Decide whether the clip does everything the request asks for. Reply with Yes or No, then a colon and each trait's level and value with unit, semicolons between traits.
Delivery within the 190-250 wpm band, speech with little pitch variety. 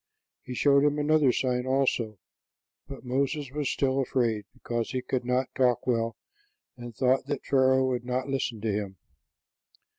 No: average, 155 wpm; narrow, 2.0 semitones